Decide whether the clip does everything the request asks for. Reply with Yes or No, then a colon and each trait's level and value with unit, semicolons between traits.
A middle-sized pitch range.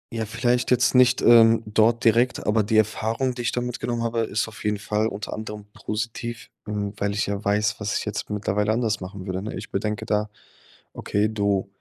No: narrow, 1.9 semitones